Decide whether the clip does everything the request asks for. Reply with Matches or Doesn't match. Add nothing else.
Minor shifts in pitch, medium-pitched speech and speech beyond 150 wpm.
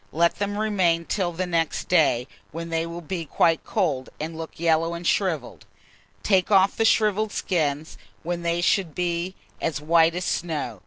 Matches